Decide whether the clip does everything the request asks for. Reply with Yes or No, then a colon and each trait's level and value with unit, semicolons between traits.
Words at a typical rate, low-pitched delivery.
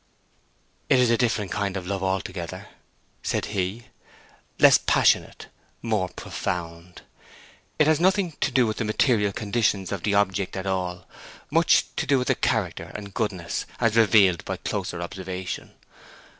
Yes: average, 150 wpm; low, 100 Hz